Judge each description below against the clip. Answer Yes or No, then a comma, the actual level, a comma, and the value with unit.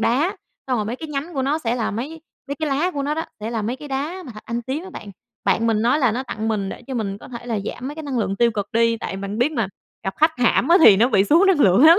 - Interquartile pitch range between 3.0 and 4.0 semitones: No, average, 5.1 semitones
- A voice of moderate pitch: No, high, 245 Hz